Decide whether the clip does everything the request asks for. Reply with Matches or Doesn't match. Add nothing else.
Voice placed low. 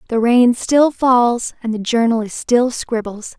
Doesn't match